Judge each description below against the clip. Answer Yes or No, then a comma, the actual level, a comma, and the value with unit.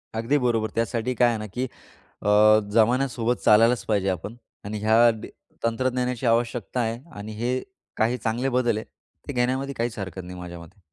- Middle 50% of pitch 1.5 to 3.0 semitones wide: Yes, narrow, 2.4 semitones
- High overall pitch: No, low, 115 Hz